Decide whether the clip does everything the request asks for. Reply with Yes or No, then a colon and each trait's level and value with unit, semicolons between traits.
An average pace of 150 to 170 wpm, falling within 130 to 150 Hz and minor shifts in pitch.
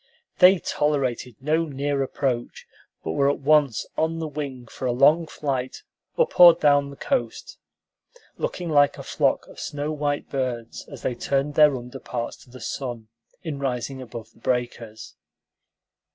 No: average, 160 wpm; medium, 140 Hz; average, 3.3 semitones